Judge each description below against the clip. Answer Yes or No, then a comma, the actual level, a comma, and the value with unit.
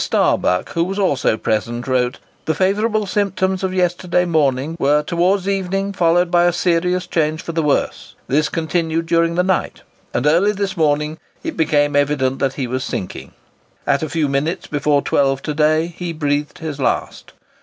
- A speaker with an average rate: Yes, average, 175 wpm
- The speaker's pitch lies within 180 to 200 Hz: No, medium, 160 Hz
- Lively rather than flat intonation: No, average, 3.8 semitones